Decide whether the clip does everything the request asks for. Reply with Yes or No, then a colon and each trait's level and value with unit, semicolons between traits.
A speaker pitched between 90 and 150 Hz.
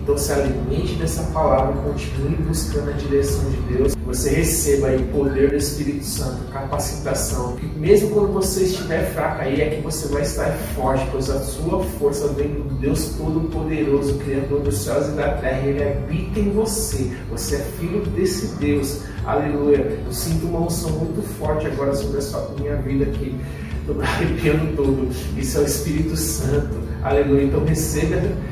Yes: medium, 140 Hz